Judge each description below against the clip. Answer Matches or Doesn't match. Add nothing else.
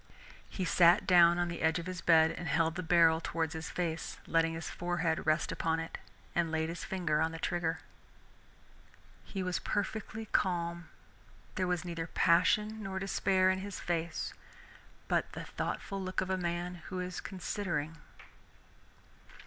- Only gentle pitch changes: Matches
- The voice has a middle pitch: Matches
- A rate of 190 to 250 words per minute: Doesn't match